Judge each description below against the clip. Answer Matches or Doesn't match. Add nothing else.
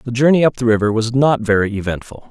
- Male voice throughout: Matches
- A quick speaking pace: Matches